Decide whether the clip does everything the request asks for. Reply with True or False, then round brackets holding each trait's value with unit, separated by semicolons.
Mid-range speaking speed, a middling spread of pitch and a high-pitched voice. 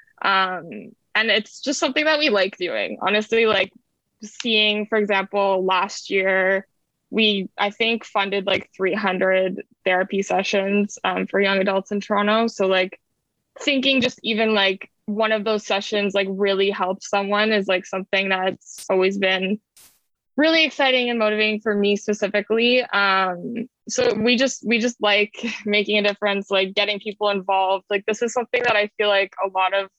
False (165 wpm; 2.3 semitones; 205 Hz)